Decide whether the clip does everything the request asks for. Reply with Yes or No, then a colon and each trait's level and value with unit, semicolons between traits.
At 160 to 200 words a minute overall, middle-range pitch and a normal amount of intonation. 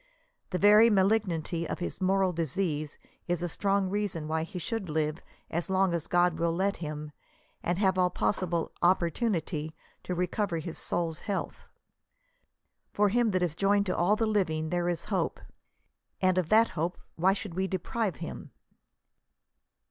Yes: average, 165 wpm; medium, 180 Hz; average, 3.1 semitones